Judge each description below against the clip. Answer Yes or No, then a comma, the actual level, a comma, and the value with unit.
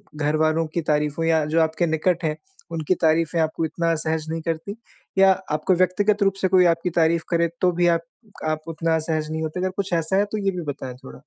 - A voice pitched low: No, medium, 165 Hz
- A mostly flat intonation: Yes, narrow, 2.3 semitones